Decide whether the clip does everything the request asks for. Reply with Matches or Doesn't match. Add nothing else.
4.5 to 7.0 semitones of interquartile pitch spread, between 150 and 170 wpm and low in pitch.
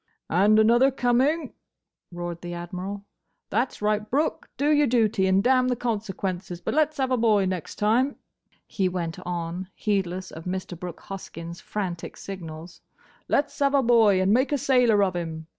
Doesn't match